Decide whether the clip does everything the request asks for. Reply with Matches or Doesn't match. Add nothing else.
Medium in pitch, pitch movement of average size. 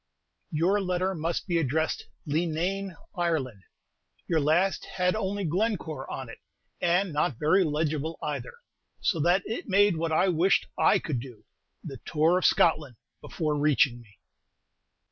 Matches